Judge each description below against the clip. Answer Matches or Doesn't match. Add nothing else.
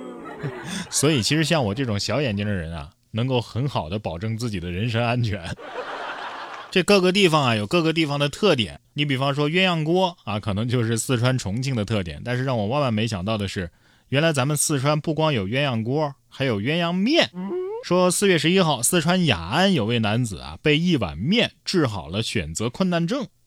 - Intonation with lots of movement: Matches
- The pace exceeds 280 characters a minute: Matches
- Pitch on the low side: Matches